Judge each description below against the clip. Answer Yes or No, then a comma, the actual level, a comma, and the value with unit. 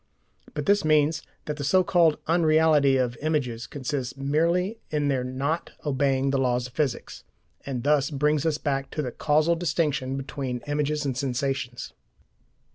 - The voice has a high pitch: No, medium, 145 Hz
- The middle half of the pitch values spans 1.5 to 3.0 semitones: Yes, average, 2.7 semitones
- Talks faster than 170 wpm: No, average, 155 wpm